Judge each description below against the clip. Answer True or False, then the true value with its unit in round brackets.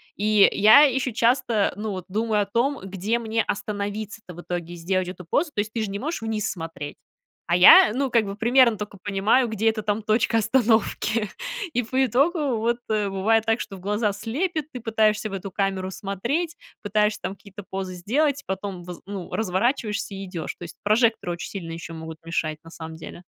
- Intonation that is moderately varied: True (3.3 semitones)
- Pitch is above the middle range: True (210 Hz)